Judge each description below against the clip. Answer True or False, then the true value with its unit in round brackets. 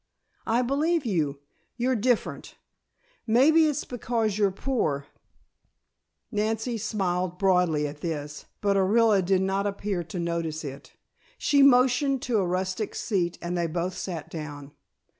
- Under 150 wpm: True (140 wpm)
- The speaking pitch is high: True (195 Hz)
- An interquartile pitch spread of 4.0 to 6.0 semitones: True (5.6 semitones)